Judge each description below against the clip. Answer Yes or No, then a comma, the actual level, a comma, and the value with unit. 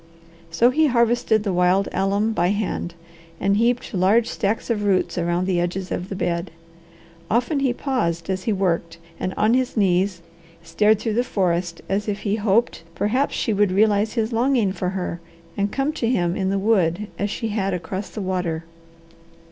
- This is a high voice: Yes, high, 200 Hz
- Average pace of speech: Yes, average, 180 wpm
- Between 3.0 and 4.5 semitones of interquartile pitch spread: Yes, average, 3.7 semitones